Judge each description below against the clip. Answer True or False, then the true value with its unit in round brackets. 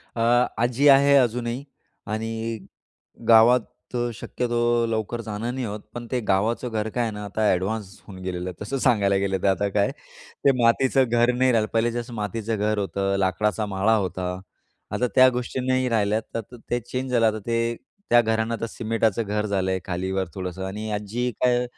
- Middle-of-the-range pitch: False (110 Hz)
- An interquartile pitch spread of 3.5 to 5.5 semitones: False (3.0 semitones)